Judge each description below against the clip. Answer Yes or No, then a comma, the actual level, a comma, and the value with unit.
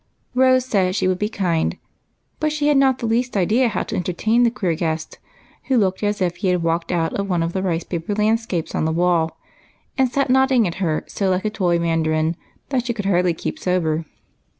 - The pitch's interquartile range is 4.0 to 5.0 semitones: No, wide, 5.5 semitones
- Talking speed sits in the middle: No, fast, 215 wpm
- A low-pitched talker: No, high, 190 Hz